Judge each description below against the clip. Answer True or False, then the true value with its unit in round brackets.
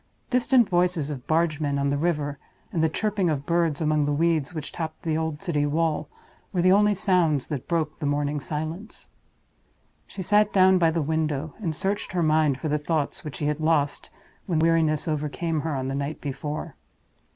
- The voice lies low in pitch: False (155 Hz)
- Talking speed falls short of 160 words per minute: False (190 wpm)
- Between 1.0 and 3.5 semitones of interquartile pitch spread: True (2.7 semitones)